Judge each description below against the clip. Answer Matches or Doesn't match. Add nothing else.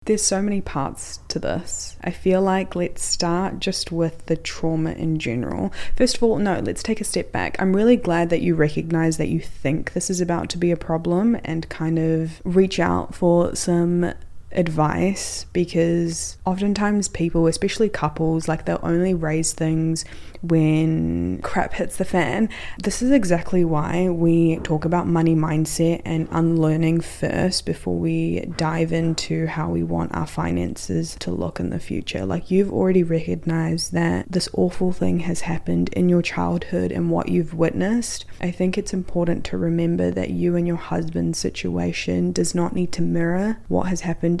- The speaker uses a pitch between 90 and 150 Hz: Doesn't match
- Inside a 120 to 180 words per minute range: Matches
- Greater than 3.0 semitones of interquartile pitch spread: Doesn't match